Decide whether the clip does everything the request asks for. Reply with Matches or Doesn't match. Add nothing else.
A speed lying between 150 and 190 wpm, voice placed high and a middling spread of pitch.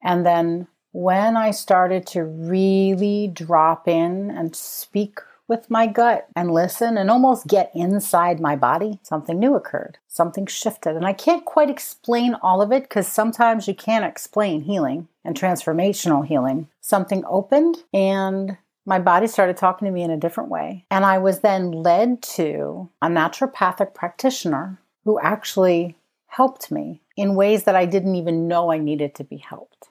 Matches